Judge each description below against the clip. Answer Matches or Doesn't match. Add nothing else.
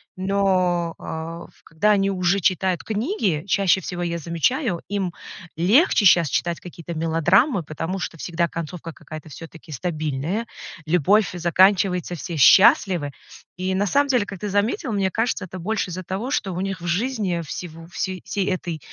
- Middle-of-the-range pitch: Matches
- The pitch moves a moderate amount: Matches